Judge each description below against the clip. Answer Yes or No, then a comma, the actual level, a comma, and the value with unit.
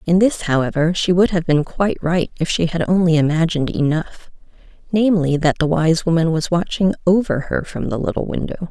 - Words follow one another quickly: No, average, 185 wpm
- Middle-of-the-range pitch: Yes, medium, 170 Hz